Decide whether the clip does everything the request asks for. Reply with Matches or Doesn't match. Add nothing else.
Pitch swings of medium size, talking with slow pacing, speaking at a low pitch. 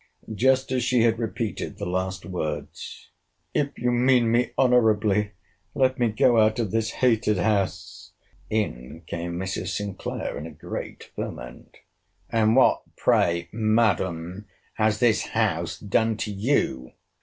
Matches